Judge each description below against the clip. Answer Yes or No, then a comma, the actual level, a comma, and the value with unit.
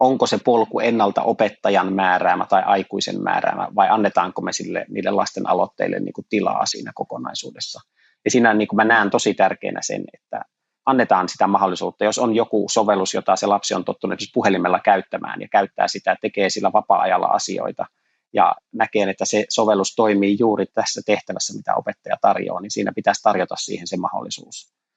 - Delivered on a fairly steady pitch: Yes, narrow, 1.9 semitones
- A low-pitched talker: Yes, low, 105 Hz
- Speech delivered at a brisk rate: Yes, fast, 170 wpm